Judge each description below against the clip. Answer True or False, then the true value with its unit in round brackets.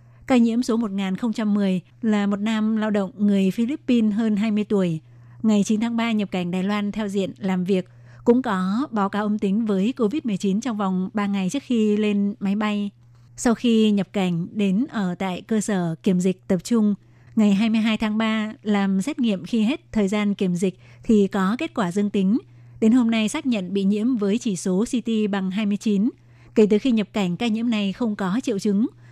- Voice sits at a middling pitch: False (205 Hz)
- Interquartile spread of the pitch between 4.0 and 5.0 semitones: False (2.5 semitones)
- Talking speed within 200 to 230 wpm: True (205 wpm)